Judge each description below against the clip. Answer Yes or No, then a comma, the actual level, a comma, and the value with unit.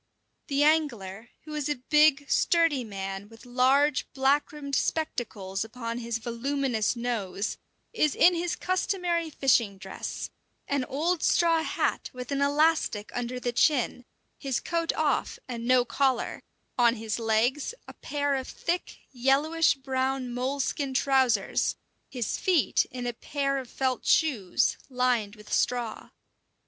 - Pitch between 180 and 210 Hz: No, very high, 260 Hz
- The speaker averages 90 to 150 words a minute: Yes, slow, 135 wpm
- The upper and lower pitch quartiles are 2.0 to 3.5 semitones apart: No, average, 3.9 semitones